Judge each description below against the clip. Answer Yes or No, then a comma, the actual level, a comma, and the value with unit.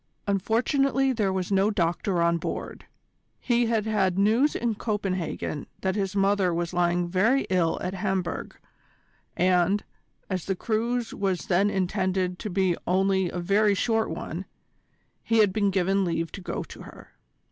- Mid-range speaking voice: No, high, 195 Hz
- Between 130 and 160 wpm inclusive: Yes, average, 155 wpm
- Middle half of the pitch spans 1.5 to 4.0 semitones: Yes, average, 2.9 semitones